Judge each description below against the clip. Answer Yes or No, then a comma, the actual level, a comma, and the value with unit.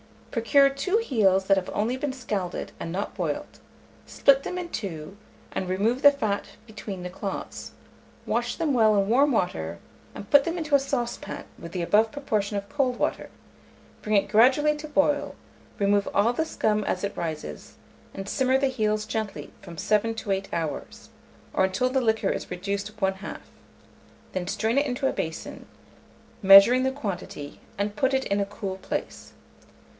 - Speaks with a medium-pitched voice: No, high, 215 Hz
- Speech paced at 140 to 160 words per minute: No, average, 175 wpm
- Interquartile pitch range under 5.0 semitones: No, average, 5.3 semitones